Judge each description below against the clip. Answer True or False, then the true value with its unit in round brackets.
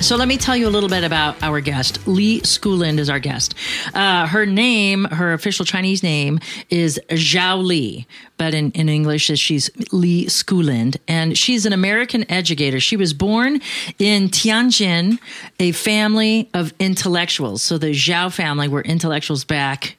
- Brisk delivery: False (160 wpm)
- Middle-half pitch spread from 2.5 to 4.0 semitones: False (4.9 semitones)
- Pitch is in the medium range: True (175 Hz)